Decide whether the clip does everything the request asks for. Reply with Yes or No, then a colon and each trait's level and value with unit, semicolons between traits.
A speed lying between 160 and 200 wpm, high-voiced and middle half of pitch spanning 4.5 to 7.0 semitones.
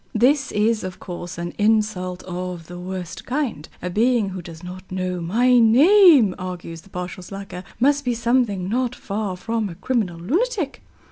Yes: average, 165 wpm; high, 200 Hz; average, 5.1 semitones